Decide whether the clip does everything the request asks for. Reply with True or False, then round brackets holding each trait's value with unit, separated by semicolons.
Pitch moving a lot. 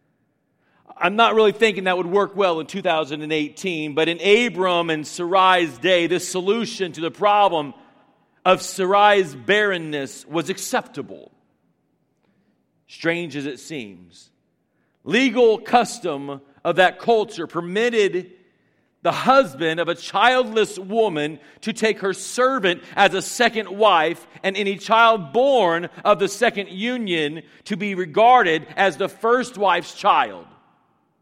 False (4.4 semitones)